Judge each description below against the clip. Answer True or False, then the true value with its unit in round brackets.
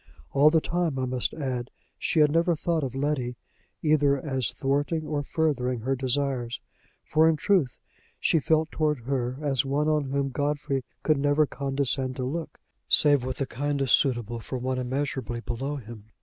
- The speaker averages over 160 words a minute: True (170 wpm)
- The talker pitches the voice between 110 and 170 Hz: True (140 Hz)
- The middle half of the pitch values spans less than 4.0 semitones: True (2.8 semitones)